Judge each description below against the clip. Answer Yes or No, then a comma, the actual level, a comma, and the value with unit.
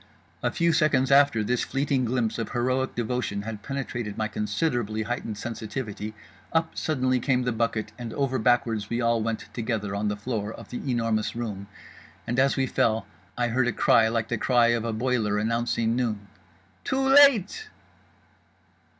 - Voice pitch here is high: No, low, 120 Hz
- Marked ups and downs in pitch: No, average, 2.9 semitones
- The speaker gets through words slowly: No, average, 165 wpm